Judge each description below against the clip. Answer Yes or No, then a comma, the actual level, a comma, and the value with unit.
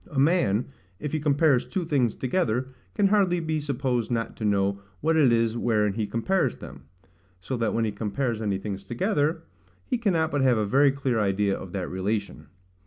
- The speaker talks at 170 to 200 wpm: Yes, average, 190 wpm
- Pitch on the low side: Yes, low, 120 Hz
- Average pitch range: No, wide, 6.3 semitones